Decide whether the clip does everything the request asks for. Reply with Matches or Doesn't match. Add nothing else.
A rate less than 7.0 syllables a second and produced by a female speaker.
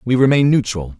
Doesn't match